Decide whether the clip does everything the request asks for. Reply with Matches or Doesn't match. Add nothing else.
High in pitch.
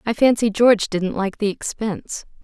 Matches